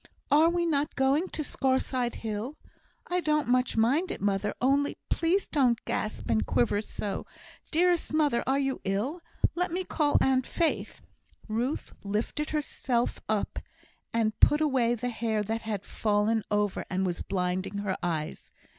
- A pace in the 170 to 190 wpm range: No, average, 155 wpm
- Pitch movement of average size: No, wide, 6.2 semitones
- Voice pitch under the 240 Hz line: No, high, 245 Hz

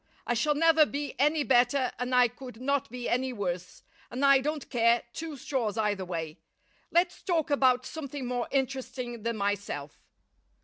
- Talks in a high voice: Yes, very high, 250 Hz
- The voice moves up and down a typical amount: Yes, average, 3.4 semitones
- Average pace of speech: Yes, average, 165 wpm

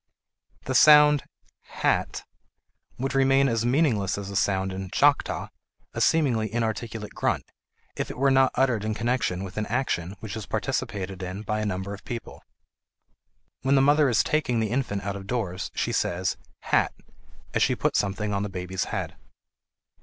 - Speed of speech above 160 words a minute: Yes, average, 175 wpm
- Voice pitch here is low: Yes, low, 110 Hz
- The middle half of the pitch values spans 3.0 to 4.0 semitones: No, average, 5.2 semitones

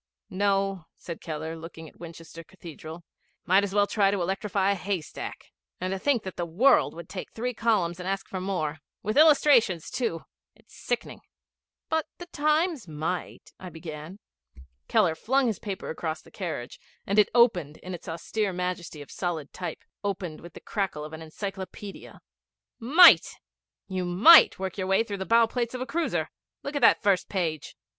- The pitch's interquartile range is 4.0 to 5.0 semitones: Yes, average, 4.5 semitones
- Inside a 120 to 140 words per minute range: No, average, 175 wpm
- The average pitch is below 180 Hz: No, high, 190 Hz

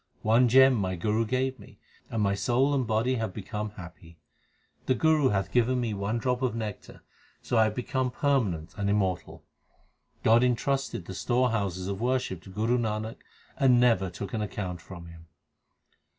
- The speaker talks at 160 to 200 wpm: Yes, average, 170 wpm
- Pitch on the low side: Yes, low, 110 Hz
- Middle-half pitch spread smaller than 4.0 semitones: No, average, 4.3 semitones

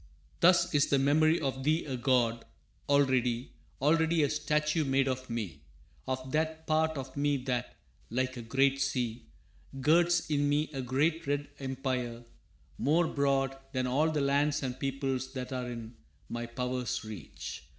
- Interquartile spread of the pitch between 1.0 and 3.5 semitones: Yes, average, 2.9 semitones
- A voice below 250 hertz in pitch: Yes, low, 135 Hz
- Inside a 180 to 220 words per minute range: No, average, 155 wpm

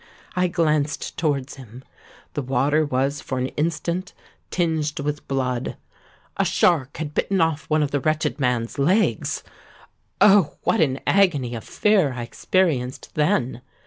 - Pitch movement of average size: Yes, average, 4.0 semitones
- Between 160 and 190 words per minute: No, average, 140 wpm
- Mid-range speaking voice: Yes, medium, 150 Hz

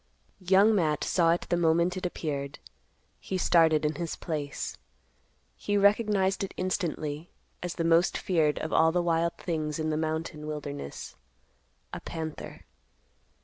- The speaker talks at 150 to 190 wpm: No, average, 140 wpm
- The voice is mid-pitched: Yes, medium, 165 Hz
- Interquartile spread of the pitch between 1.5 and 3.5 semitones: Yes, average, 2.7 semitones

